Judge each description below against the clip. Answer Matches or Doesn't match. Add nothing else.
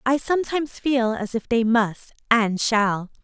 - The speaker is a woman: Matches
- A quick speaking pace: Doesn't match